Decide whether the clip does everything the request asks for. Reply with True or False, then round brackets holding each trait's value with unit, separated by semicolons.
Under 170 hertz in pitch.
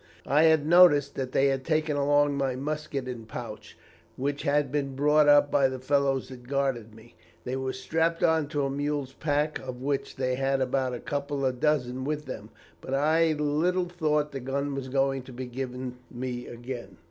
True (135 Hz)